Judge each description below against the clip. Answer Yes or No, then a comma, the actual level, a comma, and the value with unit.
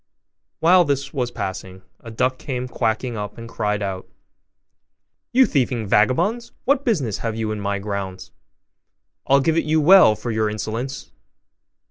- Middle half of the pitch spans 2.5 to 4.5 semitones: No, wide, 5.5 semitones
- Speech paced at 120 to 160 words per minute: Yes, average, 150 wpm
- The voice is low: Yes, low, 120 Hz